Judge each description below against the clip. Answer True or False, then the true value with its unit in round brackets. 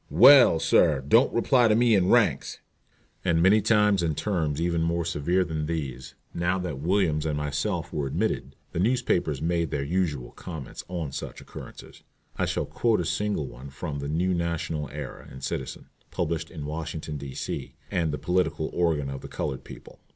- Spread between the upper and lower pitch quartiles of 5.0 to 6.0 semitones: False (3.7 semitones)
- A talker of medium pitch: False (80 Hz)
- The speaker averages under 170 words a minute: False (175 wpm)